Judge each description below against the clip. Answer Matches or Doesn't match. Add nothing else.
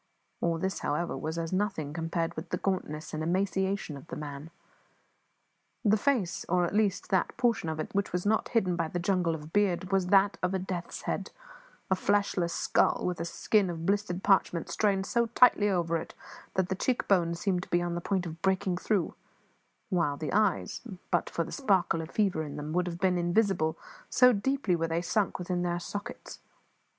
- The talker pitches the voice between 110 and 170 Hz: Doesn't match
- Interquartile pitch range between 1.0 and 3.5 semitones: Matches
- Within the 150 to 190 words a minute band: Doesn't match